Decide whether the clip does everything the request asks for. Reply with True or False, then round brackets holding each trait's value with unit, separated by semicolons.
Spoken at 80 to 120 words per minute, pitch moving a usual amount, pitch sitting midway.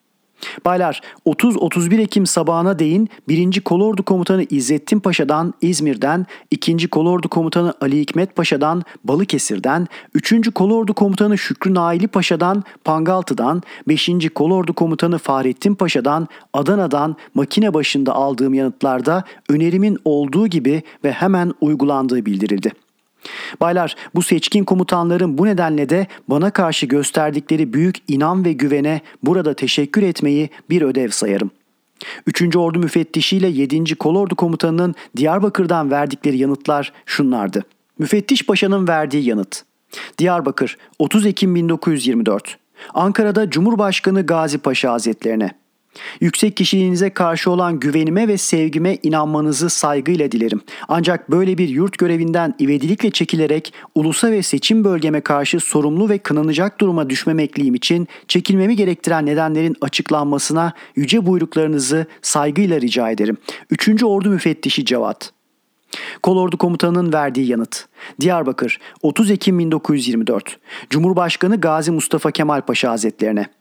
True (115 wpm; 4.1 semitones; 165 Hz)